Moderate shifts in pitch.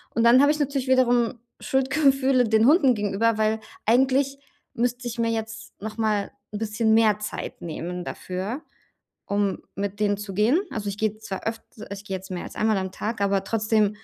Yes: average, 3.2 semitones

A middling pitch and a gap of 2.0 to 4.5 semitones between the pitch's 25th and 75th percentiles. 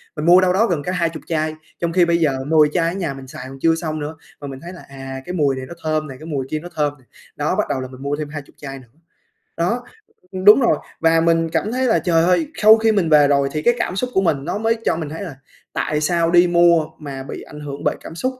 Yes: medium, 160 Hz; average, 3.3 semitones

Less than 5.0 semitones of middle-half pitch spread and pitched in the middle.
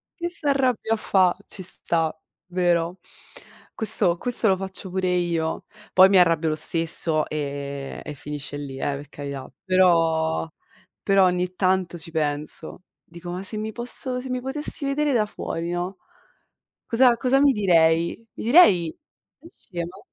No: average, 5.3 semitones; medium, 180 Hz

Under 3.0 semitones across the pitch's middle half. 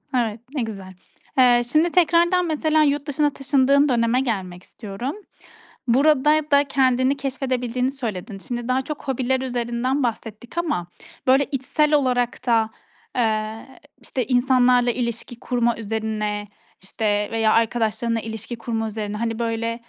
No: average, 3.3 semitones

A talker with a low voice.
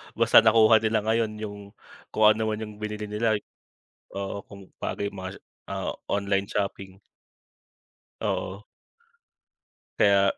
Yes: low, 105 Hz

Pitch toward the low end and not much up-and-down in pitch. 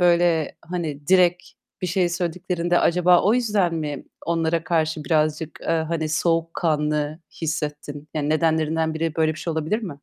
No: medium, 165 Hz; narrow, 2.0 semitones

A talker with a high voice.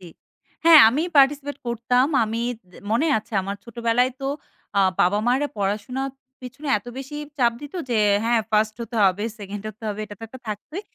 Yes: high, 235 Hz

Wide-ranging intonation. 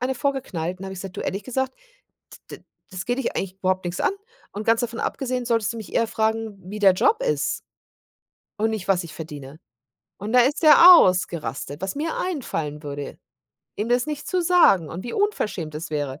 Yes: wide, 6.5 semitones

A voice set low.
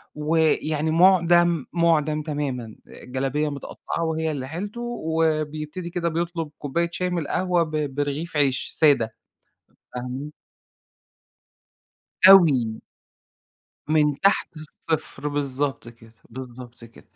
No: medium, 155 Hz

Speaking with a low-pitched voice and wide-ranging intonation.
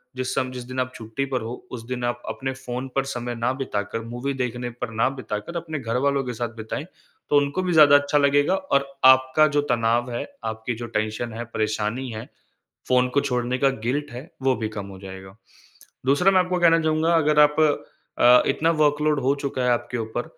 No: low, 130 Hz; average, 3.4 semitones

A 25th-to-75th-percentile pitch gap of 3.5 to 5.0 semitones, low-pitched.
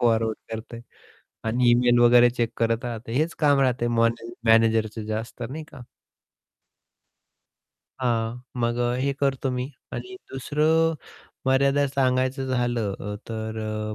No: average, 2.8 semitones; low, 120 Hz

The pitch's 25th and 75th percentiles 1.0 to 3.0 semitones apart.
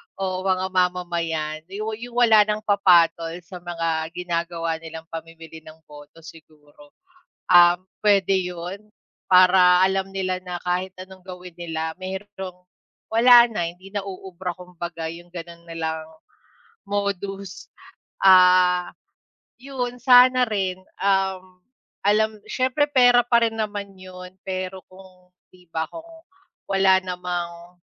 Yes: narrow, 2.5 semitones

